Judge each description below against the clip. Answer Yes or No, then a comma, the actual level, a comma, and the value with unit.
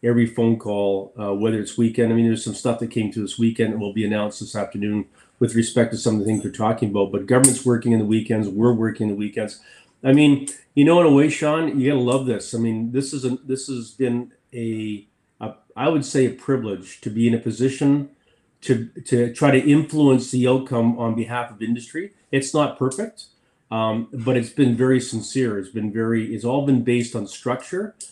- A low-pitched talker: Yes, low, 120 Hz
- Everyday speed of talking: No, fast, 220 wpm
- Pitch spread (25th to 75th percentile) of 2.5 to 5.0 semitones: Yes, average, 3.0 semitones